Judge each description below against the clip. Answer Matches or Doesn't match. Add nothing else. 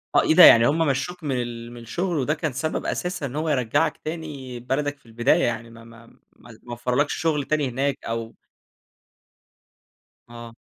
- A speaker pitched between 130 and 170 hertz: Matches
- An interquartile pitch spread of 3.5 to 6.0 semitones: Matches